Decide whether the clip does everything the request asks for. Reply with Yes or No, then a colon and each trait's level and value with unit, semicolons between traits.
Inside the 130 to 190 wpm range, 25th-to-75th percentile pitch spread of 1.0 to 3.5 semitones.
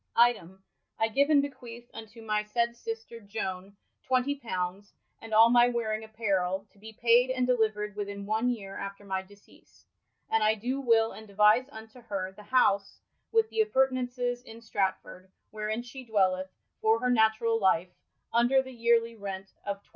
Yes: average, 160 wpm; average, 3.2 semitones